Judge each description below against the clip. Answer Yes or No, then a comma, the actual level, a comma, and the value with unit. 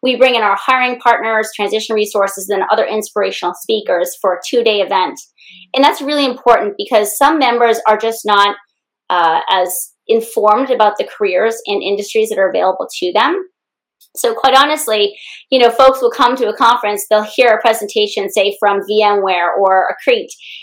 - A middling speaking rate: Yes, average, 170 wpm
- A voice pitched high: Yes, high, 220 Hz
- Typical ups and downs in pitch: Yes, average, 4.1 semitones